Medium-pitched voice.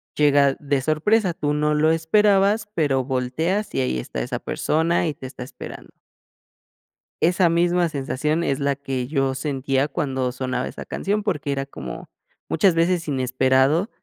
Yes: medium, 150 Hz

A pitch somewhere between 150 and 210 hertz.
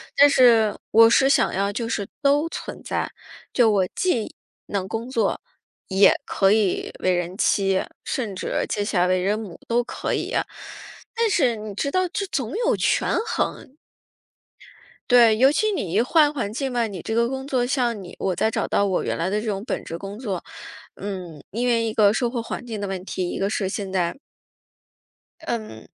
No: high, 220 Hz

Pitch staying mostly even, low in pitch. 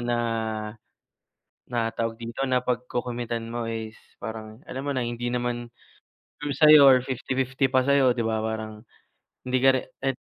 Yes: narrow, 2.2 semitones; low, 120 Hz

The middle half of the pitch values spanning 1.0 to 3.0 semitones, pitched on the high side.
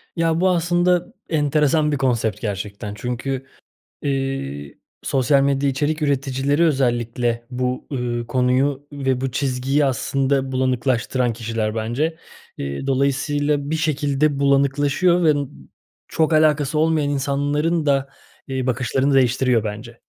No: average, 2.7 semitones; low, 135 Hz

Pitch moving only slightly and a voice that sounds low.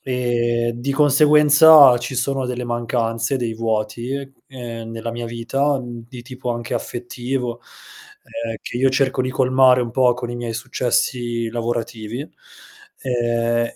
Yes: narrow, 1.9 semitones; low, 120 Hz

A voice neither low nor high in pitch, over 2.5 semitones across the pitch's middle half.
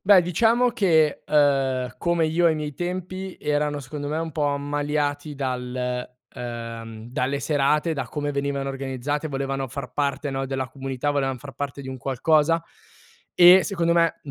Yes: medium, 145 Hz; average, 2.9 semitones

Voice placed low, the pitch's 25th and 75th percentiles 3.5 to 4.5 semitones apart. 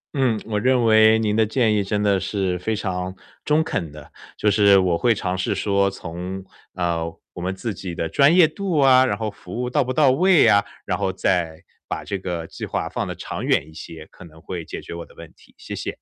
Yes: low, 100 Hz; average, 4.2 semitones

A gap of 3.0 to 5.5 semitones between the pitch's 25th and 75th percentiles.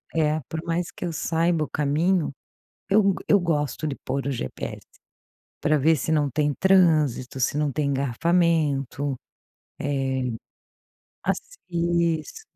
Yes: average, 3.3 semitones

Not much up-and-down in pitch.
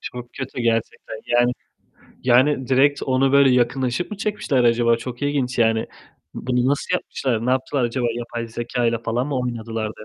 Yes: narrow, 2.1 semitones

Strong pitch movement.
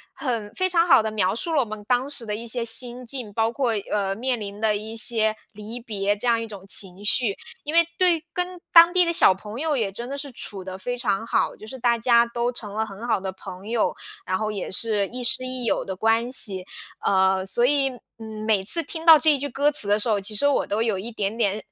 No: average, 3.8 semitones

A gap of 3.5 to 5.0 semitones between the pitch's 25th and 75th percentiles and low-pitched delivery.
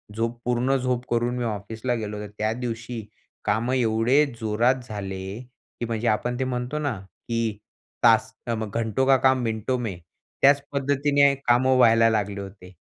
No: average, 2.7 semitones; low, 115 Hz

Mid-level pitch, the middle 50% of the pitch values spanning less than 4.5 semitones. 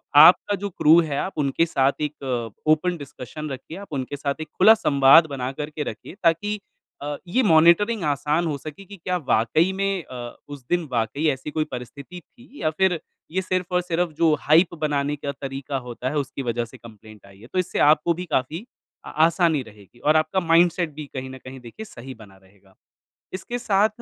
No: medium, 150 Hz; average, 4.9 semitones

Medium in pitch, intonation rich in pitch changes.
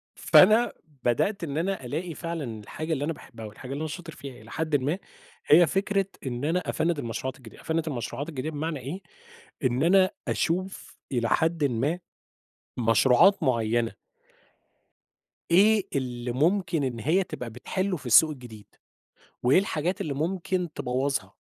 Yes: medium, 150 Hz; wide, 5.8 semitones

